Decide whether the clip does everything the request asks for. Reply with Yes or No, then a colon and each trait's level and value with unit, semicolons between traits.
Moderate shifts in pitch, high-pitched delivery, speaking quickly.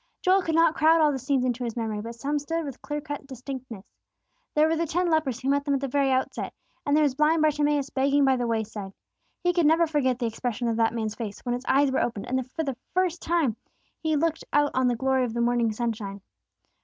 Yes: average, 4.1 semitones; very high, 270 Hz; fast, 240 wpm